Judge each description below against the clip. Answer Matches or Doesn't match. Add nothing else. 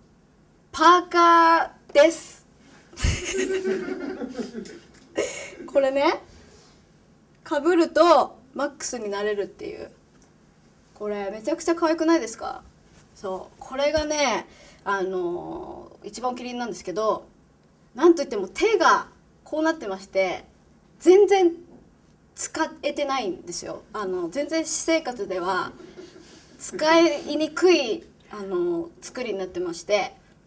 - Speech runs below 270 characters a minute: Matches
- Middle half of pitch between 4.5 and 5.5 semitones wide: Doesn't match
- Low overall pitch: Doesn't match